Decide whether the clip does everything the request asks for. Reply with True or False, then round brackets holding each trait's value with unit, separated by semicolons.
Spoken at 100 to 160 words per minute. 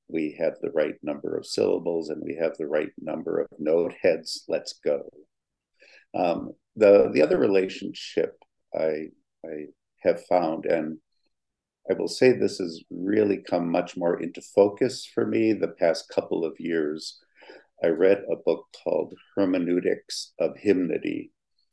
True (150 wpm)